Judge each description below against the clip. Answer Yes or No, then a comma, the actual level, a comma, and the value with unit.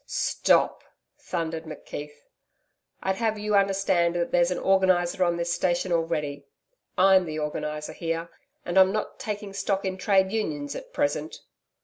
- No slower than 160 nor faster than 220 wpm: No, average, 145 wpm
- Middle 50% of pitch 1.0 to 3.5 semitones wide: Yes, average, 3.0 semitones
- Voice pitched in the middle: Yes, medium, 175 Hz